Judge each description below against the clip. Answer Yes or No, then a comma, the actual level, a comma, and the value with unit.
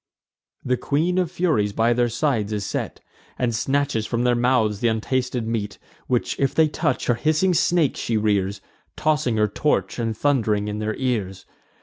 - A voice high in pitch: No, low, 120 Hz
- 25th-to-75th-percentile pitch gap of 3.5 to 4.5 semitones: No, average, 4.9 semitones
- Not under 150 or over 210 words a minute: Yes, average, 175 wpm